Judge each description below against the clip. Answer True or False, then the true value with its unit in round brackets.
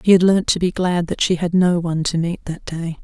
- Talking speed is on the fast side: True (295 wpm)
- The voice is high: False (175 Hz)